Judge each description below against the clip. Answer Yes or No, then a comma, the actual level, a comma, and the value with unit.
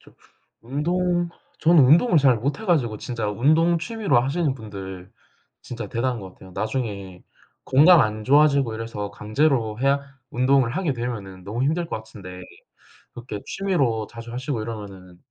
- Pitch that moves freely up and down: Yes, wide, 5.7 semitones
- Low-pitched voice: Yes, low, 120 Hz